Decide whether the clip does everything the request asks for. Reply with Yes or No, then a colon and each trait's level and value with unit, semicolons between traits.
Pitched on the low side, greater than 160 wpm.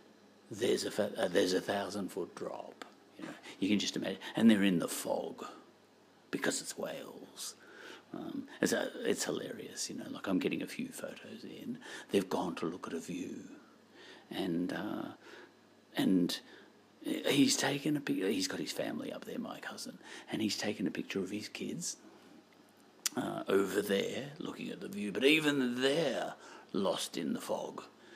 No: medium, 155 Hz; average, 170 wpm